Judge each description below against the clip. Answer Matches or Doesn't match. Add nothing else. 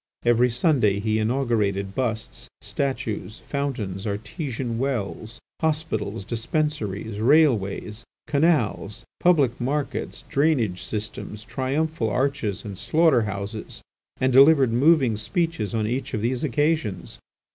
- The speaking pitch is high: Doesn't match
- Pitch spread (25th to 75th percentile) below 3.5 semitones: Doesn't match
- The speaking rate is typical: Doesn't match